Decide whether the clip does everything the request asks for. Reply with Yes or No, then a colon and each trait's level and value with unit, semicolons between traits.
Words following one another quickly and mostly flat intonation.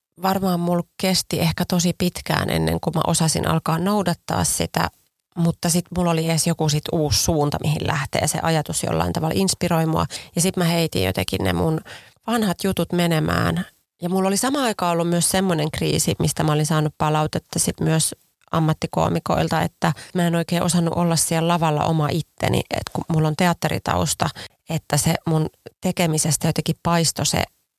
Yes: fast, 170 wpm; narrow, 2.1 semitones